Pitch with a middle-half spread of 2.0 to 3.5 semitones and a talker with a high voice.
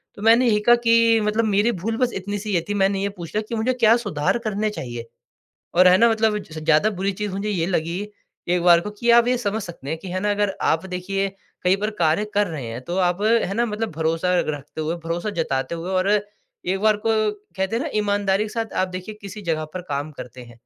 No: average, 3.9 semitones; high, 195 Hz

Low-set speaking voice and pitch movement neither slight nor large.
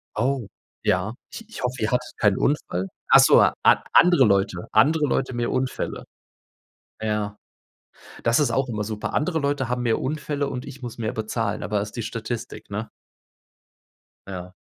Yes: low, 120 Hz; average, 4.4 semitones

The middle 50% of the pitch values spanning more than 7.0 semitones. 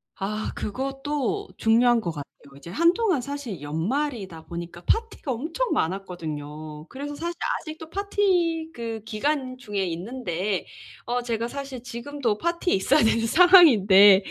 Yes: wide, 7.6 semitones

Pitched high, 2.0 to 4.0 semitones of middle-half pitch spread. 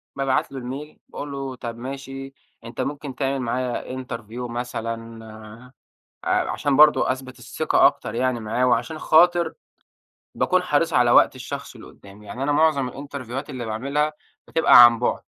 No: low, 130 Hz; average, 3.0 semitones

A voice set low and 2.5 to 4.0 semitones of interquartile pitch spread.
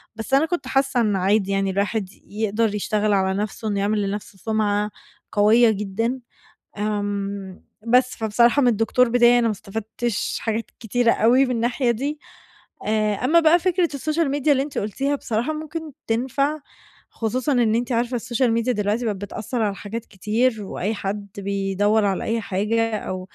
No: high, 225 Hz; average, 3.5 semitones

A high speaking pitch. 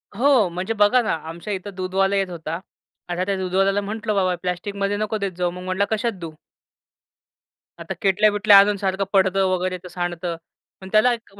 Yes: high, 195 Hz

